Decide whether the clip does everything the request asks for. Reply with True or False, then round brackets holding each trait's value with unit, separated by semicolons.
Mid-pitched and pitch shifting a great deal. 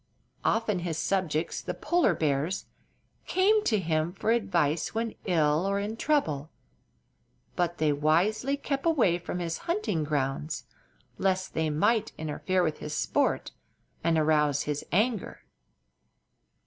True (175 Hz; 5.9 semitones)